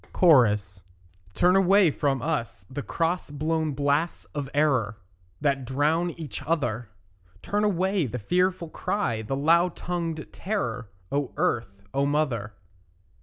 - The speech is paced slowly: Yes, slow, 125 wpm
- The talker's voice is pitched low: No, medium, 145 Hz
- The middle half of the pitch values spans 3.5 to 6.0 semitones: Yes, wide, 5.5 semitones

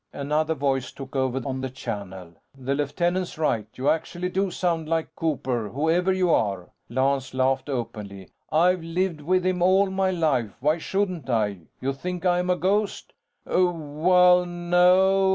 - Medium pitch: Yes, medium, 160 Hz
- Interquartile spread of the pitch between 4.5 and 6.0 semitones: Yes, wide, 5.4 semitones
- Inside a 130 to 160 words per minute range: Yes, average, 150 wpm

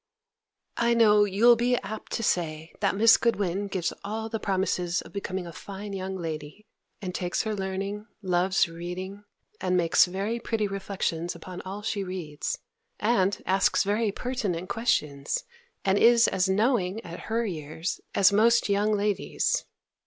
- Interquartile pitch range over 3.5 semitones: No, average, 2.9 semitones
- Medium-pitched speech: No, high, 195 Hz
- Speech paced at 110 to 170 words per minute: Yes, average, 155 wpm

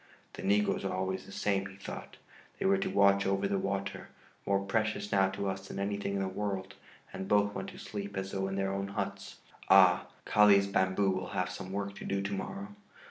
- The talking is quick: Yes, fast, 215 wpm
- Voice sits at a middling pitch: No, low, 100 Hz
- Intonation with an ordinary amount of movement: No, narrow, 0.9 semitones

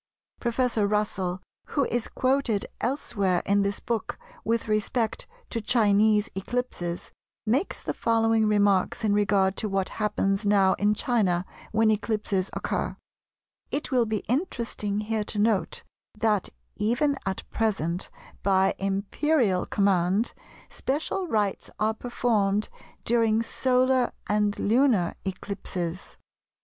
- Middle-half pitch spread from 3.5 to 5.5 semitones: No, average, 2.9 semitones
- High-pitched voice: Yes, high, 210 Hz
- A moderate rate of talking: No, slow, 115 wpm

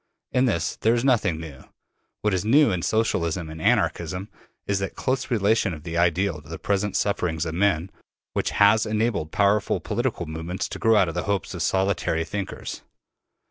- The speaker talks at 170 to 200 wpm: Yes, average, 180 wpm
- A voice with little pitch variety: No, average, 4.4 semitones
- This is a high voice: No, very low, 95 Hz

